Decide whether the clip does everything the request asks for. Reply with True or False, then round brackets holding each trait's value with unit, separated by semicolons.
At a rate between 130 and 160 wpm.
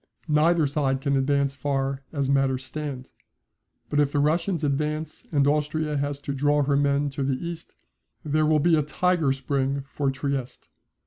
False (170 wpm)